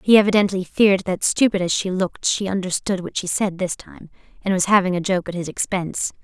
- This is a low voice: No, high, 190 Hz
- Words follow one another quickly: Yes, fast, 220 wpm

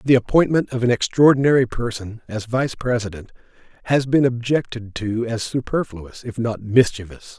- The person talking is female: No, male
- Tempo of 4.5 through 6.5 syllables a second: Yes, 5.0 syllables/s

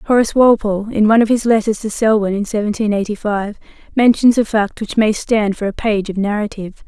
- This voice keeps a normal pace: No, fast, 210 wpm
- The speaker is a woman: Yes, female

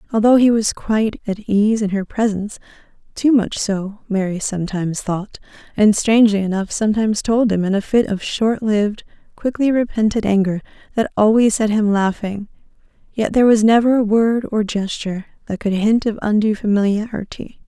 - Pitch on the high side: Yes, high, 210 Hz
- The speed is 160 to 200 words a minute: Yes, average, 165 wpm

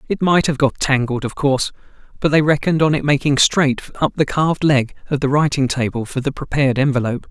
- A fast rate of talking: Yes, fast, 215 wpm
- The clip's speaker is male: Yes, male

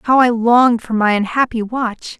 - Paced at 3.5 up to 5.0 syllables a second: Yes, 4.7 syllables/s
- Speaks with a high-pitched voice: Yes, high, 235 Hz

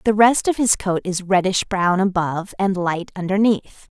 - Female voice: Yes, female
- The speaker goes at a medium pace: Yes, average, 180 wpm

